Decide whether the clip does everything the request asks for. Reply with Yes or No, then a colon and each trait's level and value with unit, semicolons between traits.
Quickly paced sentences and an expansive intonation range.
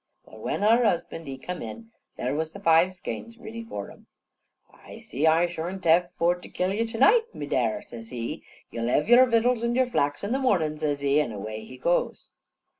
Yes: fast, 215 wpm; wide, 8.1 semitones